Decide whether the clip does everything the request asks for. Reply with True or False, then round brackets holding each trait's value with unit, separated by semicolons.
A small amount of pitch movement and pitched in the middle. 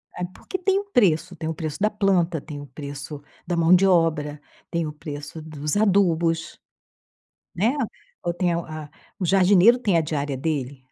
False (3.8 semitones; 165 Hz)